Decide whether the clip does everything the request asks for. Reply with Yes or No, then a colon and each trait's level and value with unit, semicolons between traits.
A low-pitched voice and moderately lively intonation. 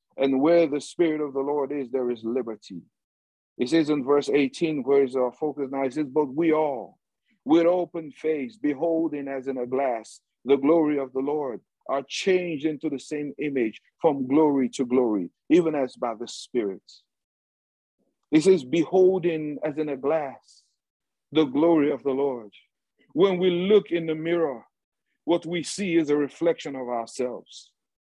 No: medium, 150 Hz; average, 3.4 semitones